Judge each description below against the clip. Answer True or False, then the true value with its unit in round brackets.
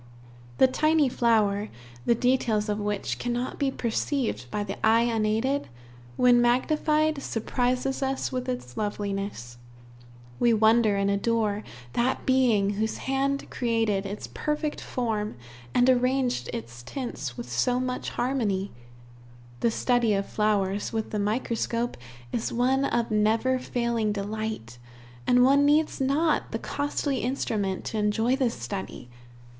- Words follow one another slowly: True (130 wpm)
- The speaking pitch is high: True (230 Hz)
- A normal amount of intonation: True (3.8 semitones)